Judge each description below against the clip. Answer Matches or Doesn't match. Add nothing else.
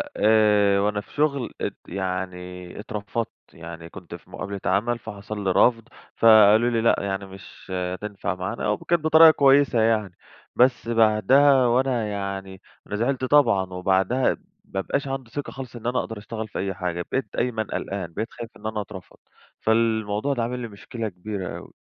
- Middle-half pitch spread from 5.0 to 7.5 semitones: Doesn't match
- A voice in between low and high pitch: Doesn't match